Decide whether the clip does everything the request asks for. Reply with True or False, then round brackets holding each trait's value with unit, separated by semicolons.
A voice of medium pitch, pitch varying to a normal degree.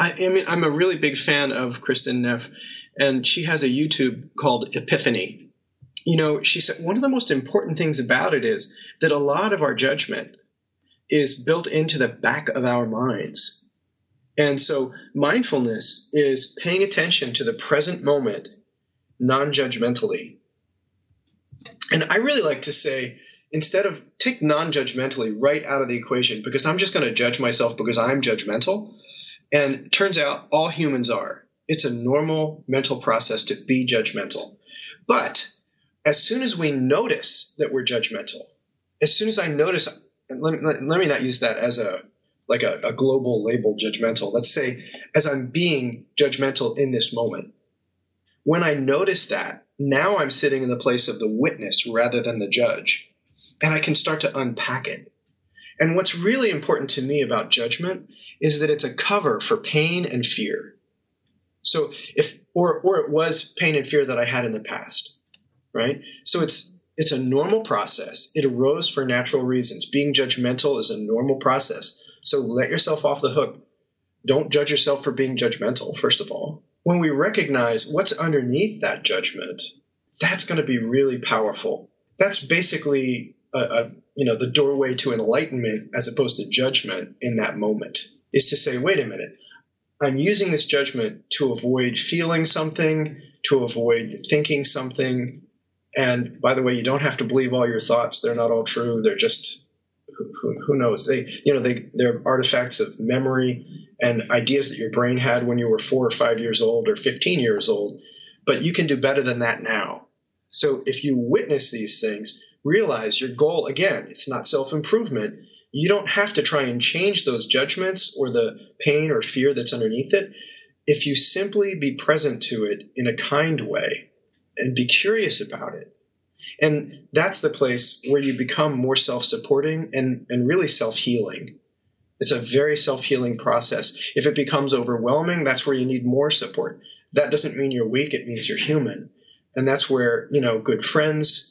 True (145 Hz; 5.0 semitones)